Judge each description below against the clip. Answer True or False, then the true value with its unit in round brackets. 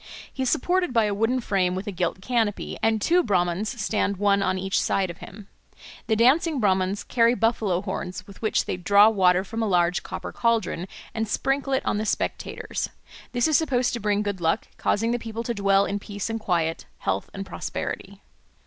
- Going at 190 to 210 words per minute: True (200 wpm)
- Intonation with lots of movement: False (3.5 semitones)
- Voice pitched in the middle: False (205 Hz)